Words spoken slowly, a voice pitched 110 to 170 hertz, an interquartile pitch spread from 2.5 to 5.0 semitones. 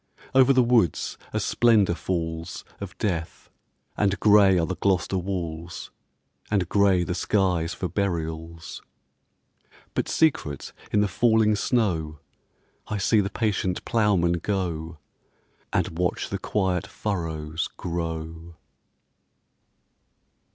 No: slow, 110 wpm; very low, 90 Hz; average, 3.8 semitones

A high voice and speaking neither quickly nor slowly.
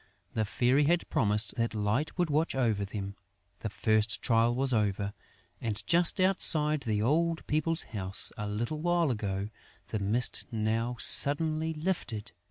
No: low, 120 Hz; average, 155 wpm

